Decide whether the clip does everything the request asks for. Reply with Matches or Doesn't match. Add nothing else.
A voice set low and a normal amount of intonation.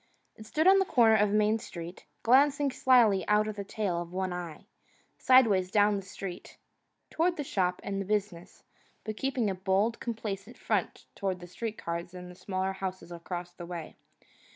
Doesn't match